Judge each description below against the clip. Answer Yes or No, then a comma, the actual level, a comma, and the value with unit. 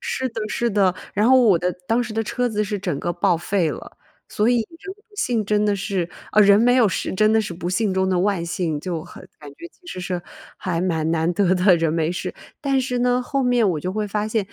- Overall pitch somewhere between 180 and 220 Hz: Yes, high, 205 Hz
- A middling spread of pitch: Yes, average, 4.7 semitones